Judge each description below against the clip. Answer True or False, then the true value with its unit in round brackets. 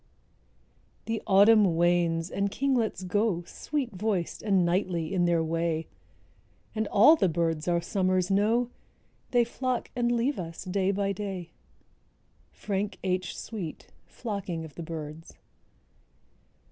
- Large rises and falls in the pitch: False (4.1 semitones)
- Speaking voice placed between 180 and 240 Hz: True (190 Hz)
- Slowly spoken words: True (130 wpm)